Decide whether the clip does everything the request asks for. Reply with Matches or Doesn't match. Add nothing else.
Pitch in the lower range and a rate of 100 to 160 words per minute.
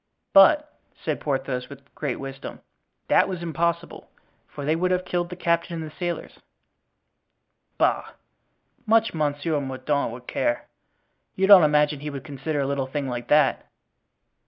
Doesn't match